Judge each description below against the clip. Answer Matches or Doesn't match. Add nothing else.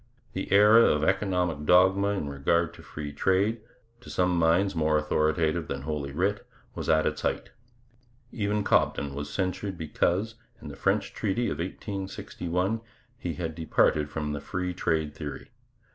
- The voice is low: Matches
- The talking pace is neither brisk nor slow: Matches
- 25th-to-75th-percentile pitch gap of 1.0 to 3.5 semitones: Doesn't match